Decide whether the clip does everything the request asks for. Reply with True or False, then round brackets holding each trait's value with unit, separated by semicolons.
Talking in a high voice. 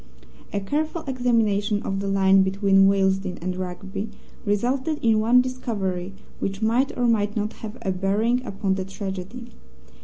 True (205 Hz)